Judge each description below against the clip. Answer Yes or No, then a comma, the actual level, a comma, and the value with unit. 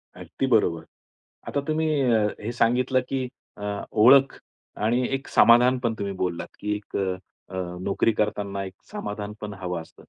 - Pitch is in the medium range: No, low, 105 Hz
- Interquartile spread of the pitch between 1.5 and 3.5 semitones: No, average, 4.0 semitones